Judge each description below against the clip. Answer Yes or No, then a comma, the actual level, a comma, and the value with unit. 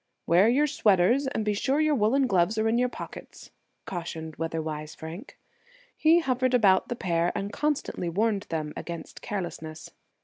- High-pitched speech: Yes, high, 205 Hz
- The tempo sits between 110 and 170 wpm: Yes, average, 165 wpm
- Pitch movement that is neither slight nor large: No, wide, 6.9 semitones